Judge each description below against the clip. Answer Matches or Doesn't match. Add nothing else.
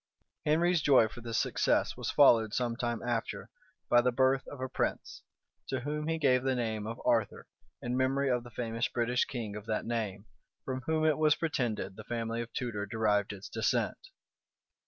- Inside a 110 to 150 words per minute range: Doesn't match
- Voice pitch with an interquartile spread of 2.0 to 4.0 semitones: Matches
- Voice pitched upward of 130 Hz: Doesn't match